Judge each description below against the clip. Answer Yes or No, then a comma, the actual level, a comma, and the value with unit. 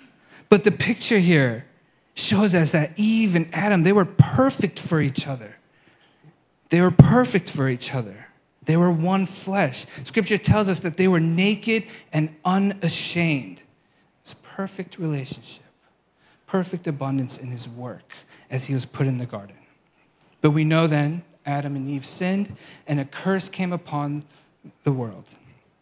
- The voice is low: No, medium, 165 Hz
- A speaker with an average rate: Yes, average, 150 wpm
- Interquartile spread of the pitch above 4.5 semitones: Yes, average, 5.2 semitones